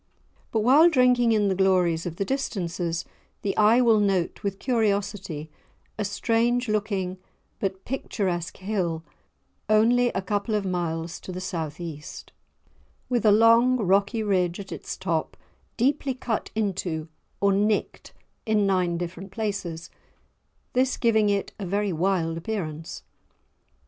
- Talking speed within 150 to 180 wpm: No, slow, 135 wpm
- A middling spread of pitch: Yes, average, 3.9 semitones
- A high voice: Yes, high, 200 Hz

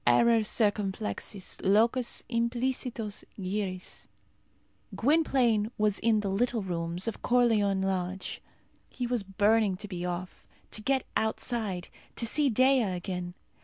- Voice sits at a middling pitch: No, high, 215 Hz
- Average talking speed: No, slow, 120 wpm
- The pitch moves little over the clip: No, average, 3.7 semitones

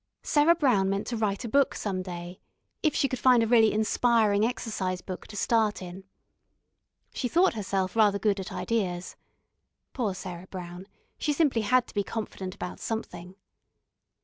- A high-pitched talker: Yes, high, 210 Hz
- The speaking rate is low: No, average, 165 wpm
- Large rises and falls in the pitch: No, average, 4.1 semitones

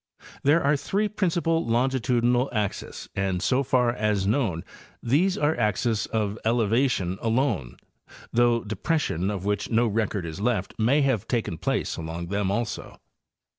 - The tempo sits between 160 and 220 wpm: No, average, 145 wpm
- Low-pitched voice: Yes, low, 115 Hz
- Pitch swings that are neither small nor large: Yes, average, 4.7 semitones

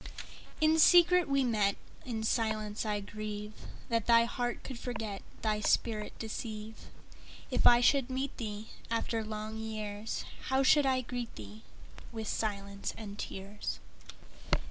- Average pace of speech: No, slow, 105 wpm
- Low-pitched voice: No, high, 220 Hz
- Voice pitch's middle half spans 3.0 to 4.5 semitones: No, narrow, 2.6 semitones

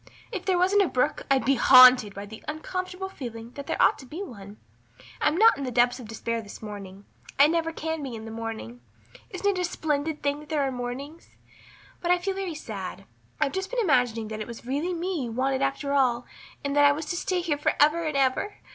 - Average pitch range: No, wide, 6.1 semitones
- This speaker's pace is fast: Yes, fast, 230 wpm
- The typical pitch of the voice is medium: No, very high, 280 Hz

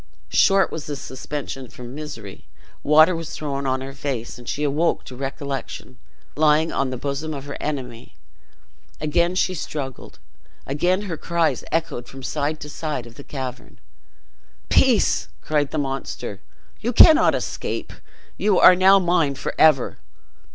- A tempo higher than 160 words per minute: No, average, 145 wpm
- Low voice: No, medium, 145 Hz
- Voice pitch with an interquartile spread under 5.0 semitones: Yes, average, 3.3 semitones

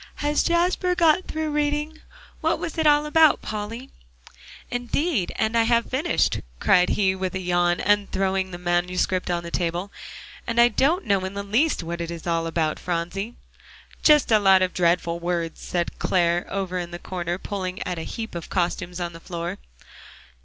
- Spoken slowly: No, average, 180 wpm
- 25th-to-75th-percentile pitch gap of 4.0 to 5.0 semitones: No, wide, 5.6 semitones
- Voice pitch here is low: No, high, 190 Hz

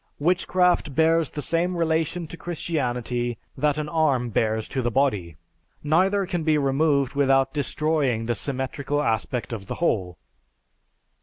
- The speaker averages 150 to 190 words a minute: No, average, 140 wpm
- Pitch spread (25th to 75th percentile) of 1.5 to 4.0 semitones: No, average, 4.8 semitones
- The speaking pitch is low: No, medium, 145 Hz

